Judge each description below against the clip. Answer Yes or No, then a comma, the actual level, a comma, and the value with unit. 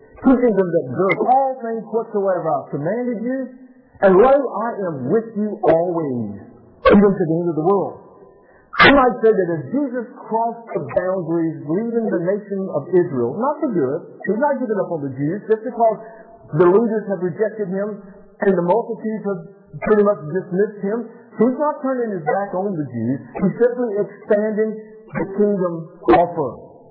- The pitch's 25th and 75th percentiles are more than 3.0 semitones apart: Yes, average, 4.0 semitones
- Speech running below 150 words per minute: No, average, 175 wpm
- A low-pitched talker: No, high, 205 Hz